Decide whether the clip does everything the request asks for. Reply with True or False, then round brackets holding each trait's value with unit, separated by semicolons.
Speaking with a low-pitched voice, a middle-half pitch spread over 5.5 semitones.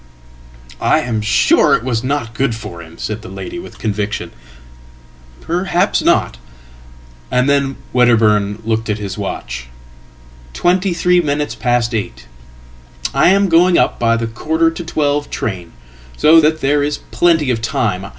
True (120 Hz; 7.0 semitones)